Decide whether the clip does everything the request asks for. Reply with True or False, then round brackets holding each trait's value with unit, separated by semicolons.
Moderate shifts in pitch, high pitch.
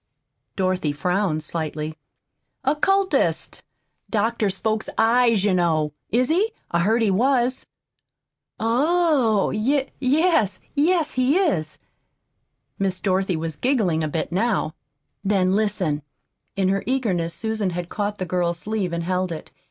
False (6.0 semitones; 205 Hz)